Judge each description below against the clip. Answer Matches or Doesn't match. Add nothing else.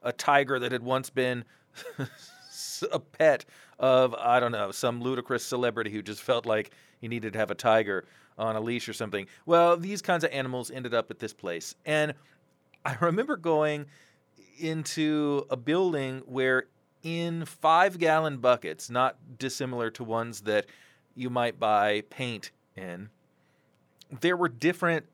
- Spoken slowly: Doesn't match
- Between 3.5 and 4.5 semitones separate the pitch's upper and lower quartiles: Doesn't match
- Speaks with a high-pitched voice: Doesn't match